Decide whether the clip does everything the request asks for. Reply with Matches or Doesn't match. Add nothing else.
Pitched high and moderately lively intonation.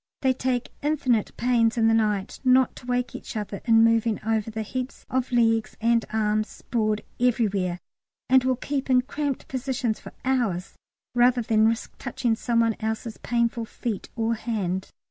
Doesn't match